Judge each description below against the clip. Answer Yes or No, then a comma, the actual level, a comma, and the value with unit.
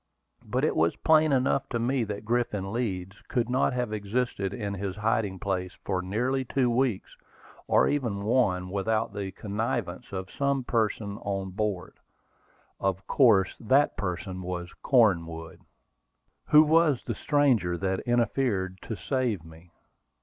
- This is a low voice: Yes, low, 105 Hz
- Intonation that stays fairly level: No, average, 4.7 semitones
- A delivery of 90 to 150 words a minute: Yes, average, 140 wpm